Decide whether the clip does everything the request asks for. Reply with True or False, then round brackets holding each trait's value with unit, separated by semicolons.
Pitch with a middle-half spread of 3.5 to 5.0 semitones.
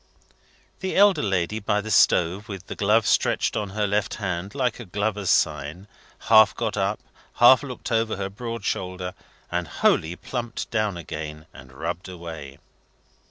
True (3.9 semitones)